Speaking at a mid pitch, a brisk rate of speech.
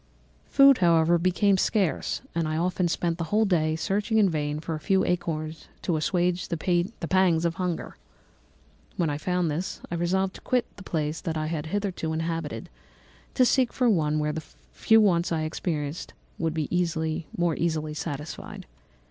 No: medium, 170 Hz; average, 170 wpm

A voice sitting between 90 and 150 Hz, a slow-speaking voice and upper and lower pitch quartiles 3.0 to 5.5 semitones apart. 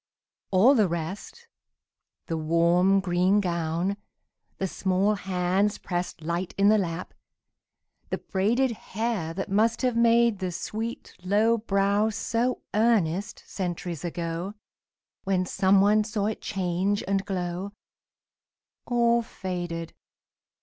No: high, 195 Hz; slow, 115 wpm; average, 3.3 semitones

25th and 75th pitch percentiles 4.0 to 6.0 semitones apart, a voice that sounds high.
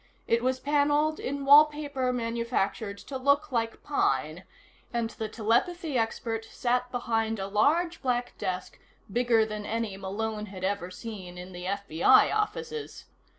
Yes: average, 5.0 semitones; high, 230 Hz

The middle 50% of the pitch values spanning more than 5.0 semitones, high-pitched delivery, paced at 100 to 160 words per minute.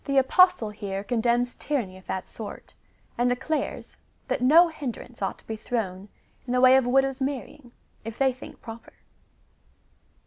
No: average, 3.5 semitones; high, 245 Hz; average, 150 wpm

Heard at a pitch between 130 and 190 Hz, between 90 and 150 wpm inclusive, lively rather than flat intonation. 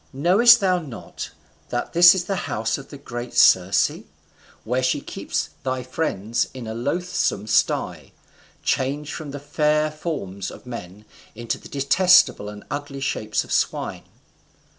Yes: low, 135 Hz; average, 140 wpm; wide, 6.0 semitones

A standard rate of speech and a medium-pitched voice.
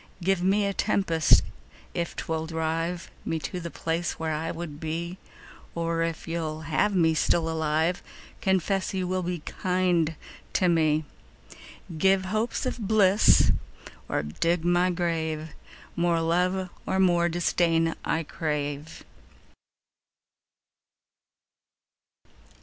No: slow, 120 wpm; medium, 170 Hz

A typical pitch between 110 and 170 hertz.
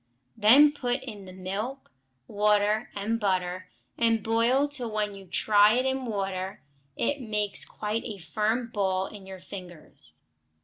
No: high, 210 Hz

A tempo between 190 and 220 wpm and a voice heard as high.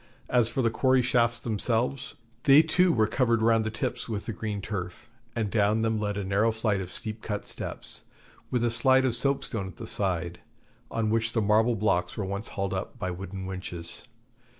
No: average, 200 wpm; low, 110 Hz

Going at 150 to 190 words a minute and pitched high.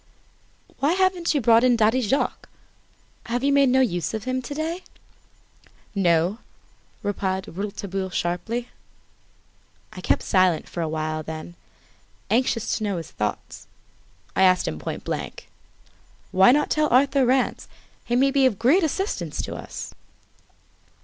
No: average, 140 wpm; high, 230 Hz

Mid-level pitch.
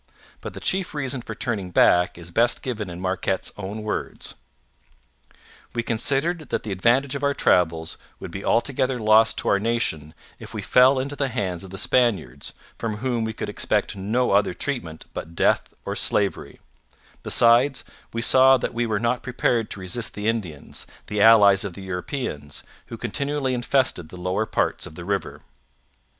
No: low, 110 Hz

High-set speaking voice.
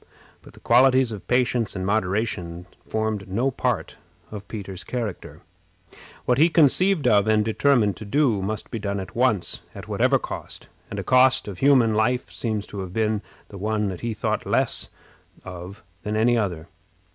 No: low, 110 Hz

